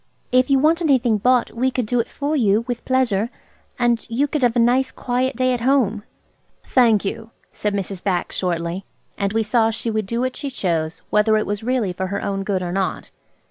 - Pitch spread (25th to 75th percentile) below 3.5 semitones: No, average, 4.2 semitones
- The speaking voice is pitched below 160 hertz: No, high, 230 Hz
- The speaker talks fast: Yes, fast, 215 wpm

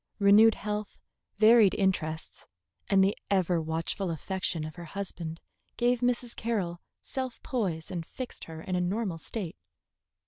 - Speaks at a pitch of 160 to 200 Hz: Yes, high, 190 Hz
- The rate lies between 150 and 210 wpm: No, average, 140 wpm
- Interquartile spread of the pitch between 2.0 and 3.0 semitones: No, average, 4.6 semitones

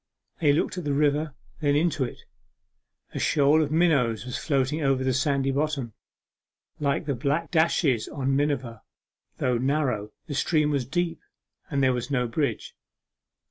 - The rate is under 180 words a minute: Yes, average, 155 wpm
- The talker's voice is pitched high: No, medium, 140 Hz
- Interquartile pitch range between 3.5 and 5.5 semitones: No, average, 2.8 semitones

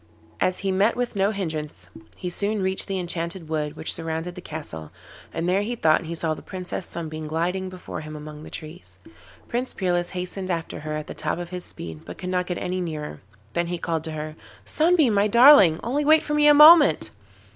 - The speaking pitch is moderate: Yes, medium, 180 Hz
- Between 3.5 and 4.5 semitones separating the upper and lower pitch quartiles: Yes, average, 3.9 semitones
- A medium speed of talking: No, fast, 210 wpm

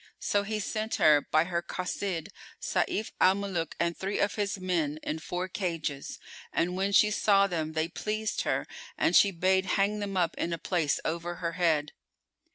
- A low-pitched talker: No, medium, 180 Hz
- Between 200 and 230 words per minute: No, average, 180 wpm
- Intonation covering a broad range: No, average, 3.2 semitones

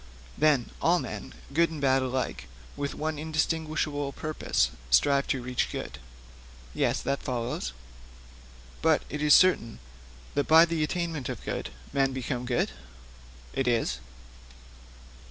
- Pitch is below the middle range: No, medium, 145 Hz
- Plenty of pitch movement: No, average, 3.3 semitones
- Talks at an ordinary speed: No, slow, 130 wpm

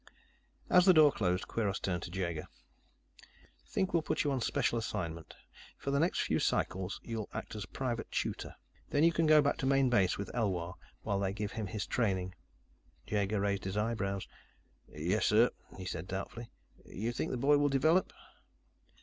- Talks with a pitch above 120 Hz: No, low, 105 Hz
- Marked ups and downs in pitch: Yes, wide, 6.0 semitones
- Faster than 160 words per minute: Yes, average, 180 wpm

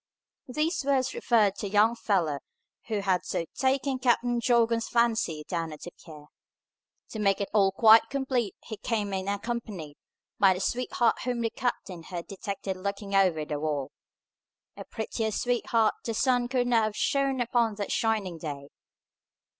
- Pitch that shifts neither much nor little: Yes, average, 4.1 semitones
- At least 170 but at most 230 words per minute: No, average, 160 wpm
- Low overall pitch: No, high, 215 Hz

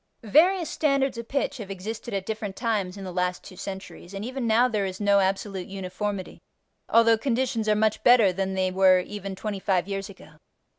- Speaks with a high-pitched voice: Yes, high, 200 Hz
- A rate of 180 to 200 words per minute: Yes, average, 195 wpm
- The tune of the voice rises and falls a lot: No, average, 3.2 semitones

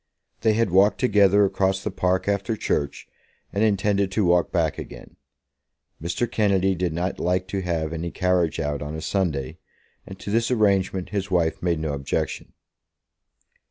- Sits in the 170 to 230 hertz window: No, very low, 95 Hz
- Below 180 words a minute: Yes, average, 160 wpm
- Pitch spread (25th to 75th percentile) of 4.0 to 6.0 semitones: No, average, 2.8 semitones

